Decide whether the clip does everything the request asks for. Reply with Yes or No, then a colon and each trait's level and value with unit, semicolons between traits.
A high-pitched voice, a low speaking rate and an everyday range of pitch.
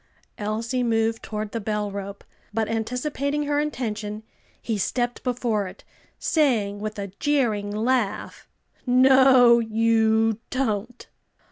Yes: high, 225 Hz; slow, 115 wpm; average, 3.0 semitones